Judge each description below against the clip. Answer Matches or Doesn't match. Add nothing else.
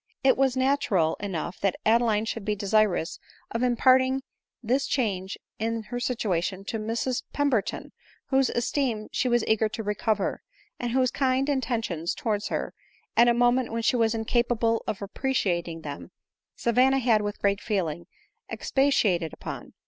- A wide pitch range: Doesn't match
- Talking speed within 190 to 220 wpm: Doesn't match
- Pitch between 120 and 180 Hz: Doesn't match